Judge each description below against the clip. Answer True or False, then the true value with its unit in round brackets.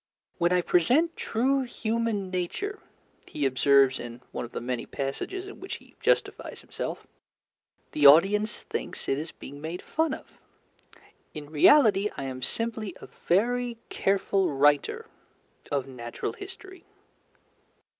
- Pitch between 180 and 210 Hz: True (185 Hz)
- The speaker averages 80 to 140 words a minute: True (135 wpm)